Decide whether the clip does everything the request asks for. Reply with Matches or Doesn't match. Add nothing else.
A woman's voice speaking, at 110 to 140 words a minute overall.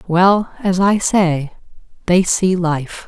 Matches